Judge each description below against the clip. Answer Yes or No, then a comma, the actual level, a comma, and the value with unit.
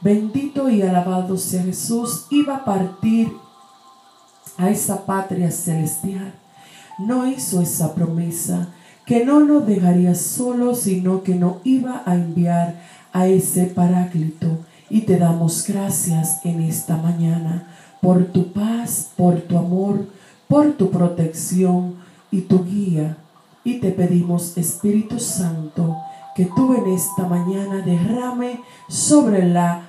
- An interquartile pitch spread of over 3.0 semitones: No, average, 2.7 semitones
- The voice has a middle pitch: Yes, medium, 180 Hz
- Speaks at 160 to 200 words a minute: No, slow, 125 wpm